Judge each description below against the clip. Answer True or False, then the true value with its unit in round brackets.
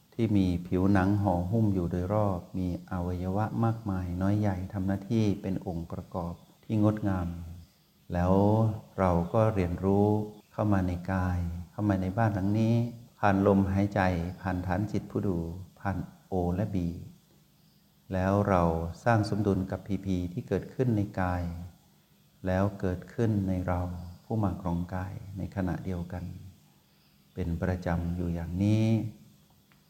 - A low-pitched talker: True (95 Hz)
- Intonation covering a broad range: False (2.6 semitones)